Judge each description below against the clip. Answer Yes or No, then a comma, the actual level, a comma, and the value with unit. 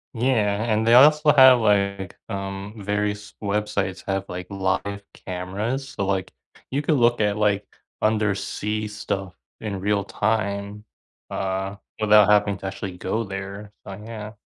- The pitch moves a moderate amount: No, narrow, 1.7 semitones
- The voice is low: Yes, low, 105 Hz